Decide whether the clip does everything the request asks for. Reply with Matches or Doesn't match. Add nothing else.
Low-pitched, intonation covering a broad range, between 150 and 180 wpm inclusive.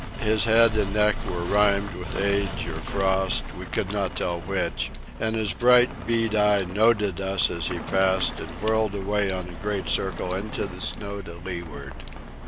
Doesn't match